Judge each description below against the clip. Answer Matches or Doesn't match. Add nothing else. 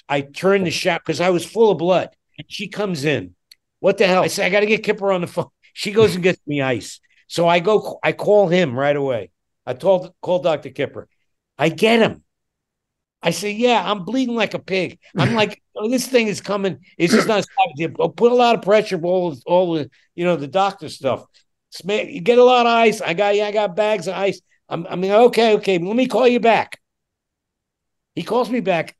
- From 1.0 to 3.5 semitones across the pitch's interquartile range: Doesn't match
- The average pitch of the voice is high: Matches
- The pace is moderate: Doesn't match